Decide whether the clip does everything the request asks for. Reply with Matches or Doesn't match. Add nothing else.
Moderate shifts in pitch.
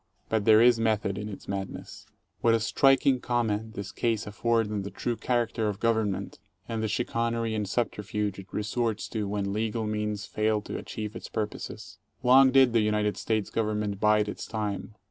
Doesn't match